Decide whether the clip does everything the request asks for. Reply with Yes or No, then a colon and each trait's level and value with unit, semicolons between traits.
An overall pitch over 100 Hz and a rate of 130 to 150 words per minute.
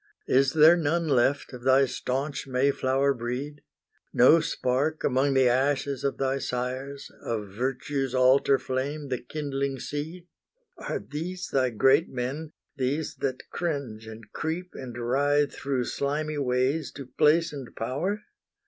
Yes: low, 135 Hz; average, 140 wpm